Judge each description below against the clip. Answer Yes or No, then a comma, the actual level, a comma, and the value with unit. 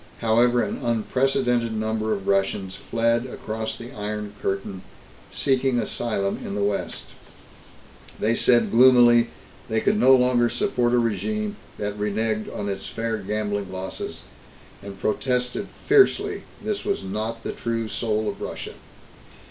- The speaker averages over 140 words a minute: No, slow, 135 wpm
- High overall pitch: No, low, 115 Hz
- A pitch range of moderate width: Yes, average, 3.0 semitones